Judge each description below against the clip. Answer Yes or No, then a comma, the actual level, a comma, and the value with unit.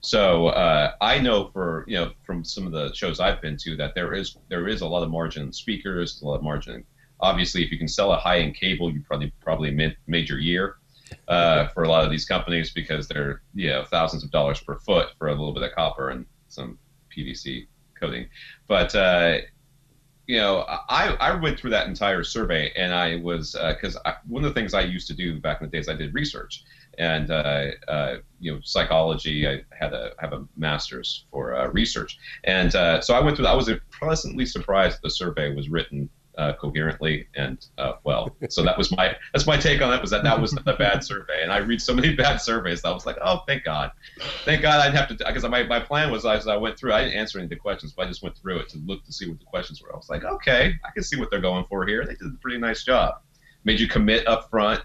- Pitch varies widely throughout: Yes, wide, 6.3 semitones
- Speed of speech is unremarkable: No, fast, 245 wpm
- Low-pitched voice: Yes, very low, 85 Hz